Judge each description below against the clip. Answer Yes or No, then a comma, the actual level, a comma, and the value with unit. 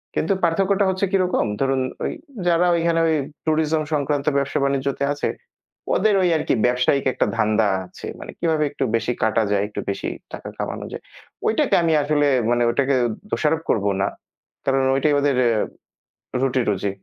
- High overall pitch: No, medium, 140 Hz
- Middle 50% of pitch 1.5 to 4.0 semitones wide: No, average, 4.5 semitones